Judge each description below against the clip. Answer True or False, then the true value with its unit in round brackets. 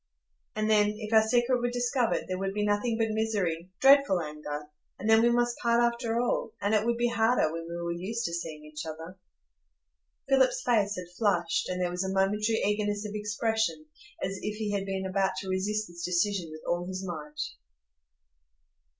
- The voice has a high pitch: True (205 Hz)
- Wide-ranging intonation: False (4.0 semitones)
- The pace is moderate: True (190 wpm)